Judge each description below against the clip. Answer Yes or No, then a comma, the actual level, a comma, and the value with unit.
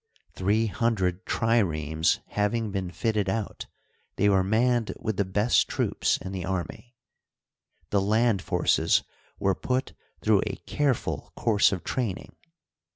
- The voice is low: Yes, low, 105 Hz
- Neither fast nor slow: No, slow, 130 wpm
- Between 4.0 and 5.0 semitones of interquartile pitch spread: No, average, 3.2 semitones